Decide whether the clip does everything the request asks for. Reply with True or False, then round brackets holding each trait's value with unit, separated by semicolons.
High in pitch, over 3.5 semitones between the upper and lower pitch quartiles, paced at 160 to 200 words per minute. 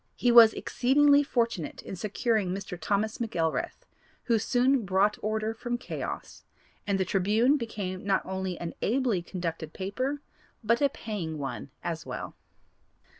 False (210 Hz; 4.4 semitones; 140 wpm)